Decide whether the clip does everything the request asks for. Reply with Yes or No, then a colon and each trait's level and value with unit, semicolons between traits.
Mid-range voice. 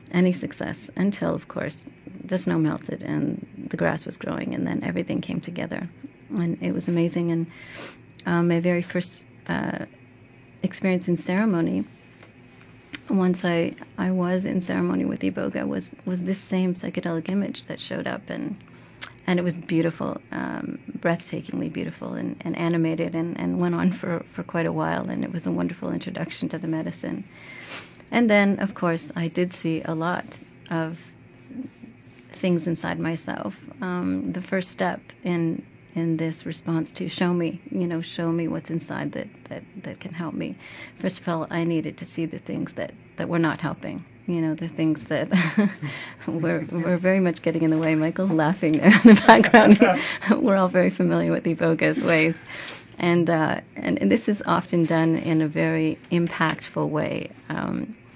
Yes: medium, 170 Hz